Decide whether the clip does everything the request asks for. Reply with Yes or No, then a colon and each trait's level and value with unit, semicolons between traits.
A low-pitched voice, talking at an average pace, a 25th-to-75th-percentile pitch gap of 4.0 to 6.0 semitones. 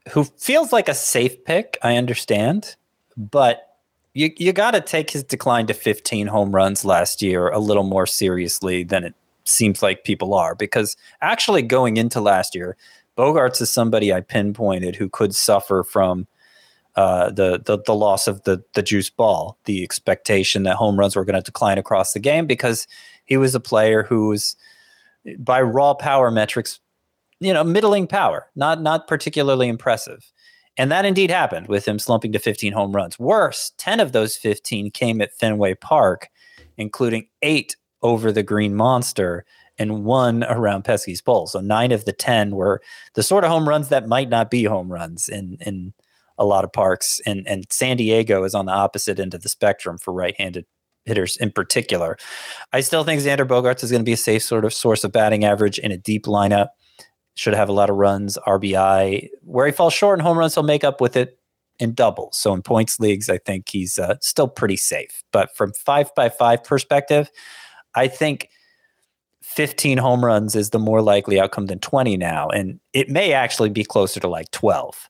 Yes: low, 110 Hz; average, 190 wpm; wide, 5.5 semitones